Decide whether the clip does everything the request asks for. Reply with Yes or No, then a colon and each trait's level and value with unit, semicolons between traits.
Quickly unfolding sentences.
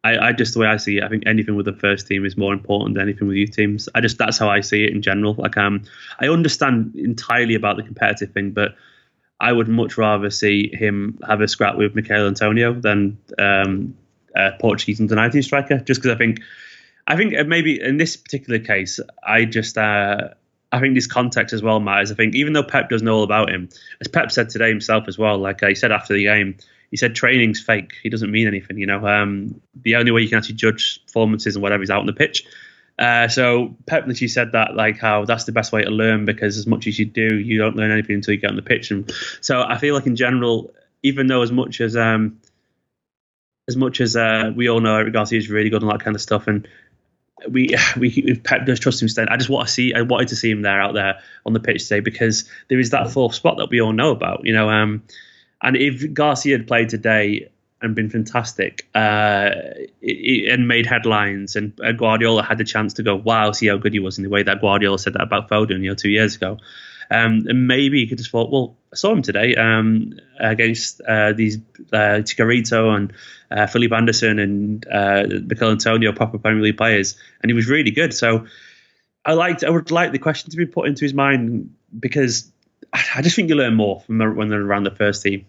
Yes: fast, 235 wpm